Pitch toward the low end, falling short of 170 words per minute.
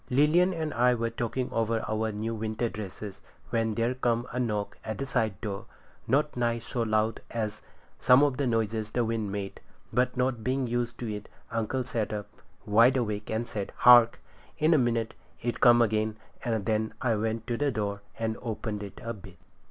No: low, 115 Hz; average, 190 wpm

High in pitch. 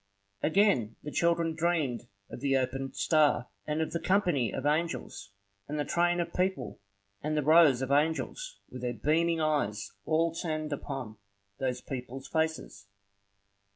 No: medium, 150 Hz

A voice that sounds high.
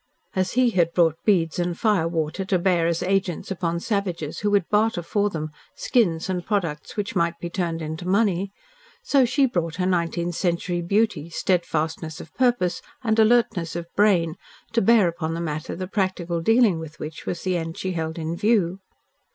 No: medium, 175 Hz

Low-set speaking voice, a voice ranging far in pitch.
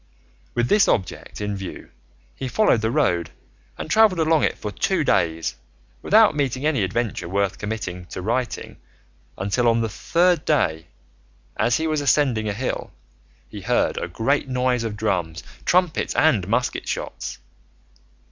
Yes: low, 120 Hz; wide, 6.8 semitones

